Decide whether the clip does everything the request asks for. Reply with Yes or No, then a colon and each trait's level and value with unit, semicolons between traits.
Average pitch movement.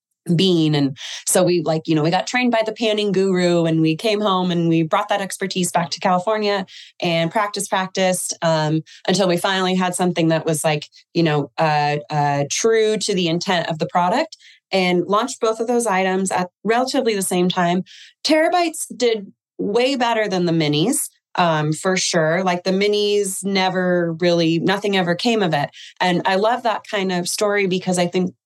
Yes: average, 3.6 semitones